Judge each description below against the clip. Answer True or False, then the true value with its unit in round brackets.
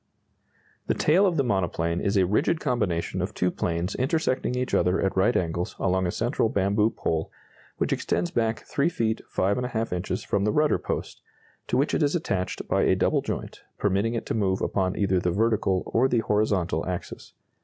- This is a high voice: False (100 Hz)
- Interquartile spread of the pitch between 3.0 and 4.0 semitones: False (5.0 semitones)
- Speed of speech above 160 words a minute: True (190 wpm)